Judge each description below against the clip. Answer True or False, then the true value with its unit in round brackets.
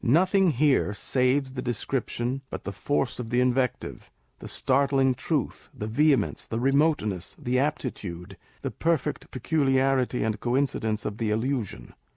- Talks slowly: False (145 wpm)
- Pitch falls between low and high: False (130 Hz)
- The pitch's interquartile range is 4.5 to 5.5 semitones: False (3.4 semitones)